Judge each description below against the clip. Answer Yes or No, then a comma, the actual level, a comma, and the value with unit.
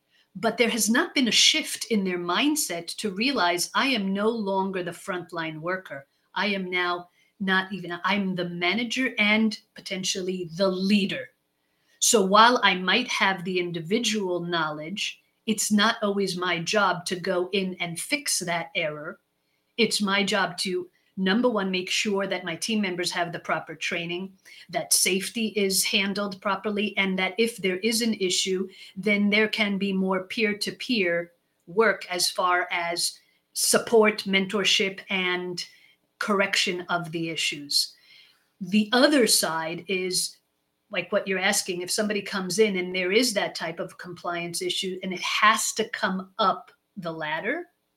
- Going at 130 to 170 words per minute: Yes, average, 160 wpm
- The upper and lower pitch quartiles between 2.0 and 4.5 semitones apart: Yes, average, 3.0 semitones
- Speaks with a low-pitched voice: No, high, 190 Hz